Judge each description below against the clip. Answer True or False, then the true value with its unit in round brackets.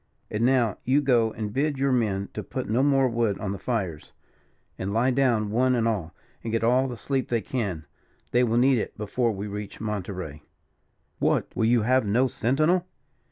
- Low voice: True (115 Hz)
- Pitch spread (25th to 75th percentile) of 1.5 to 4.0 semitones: True (3.6 semitones)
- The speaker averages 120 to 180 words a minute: False (195 wpm)